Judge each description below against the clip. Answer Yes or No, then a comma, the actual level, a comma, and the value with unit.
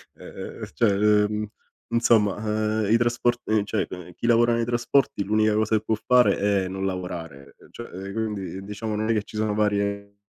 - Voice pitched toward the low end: Yes, low, 105 Hz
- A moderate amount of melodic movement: No, narrow, 1.8 semitones